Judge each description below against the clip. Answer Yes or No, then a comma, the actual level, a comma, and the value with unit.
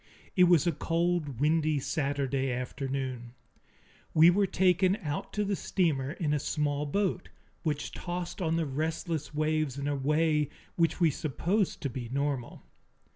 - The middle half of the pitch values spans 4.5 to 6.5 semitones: No, average, 3.7 semitones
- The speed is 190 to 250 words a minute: No, average, 150 wpm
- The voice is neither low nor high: Yes, medium, 155 Hz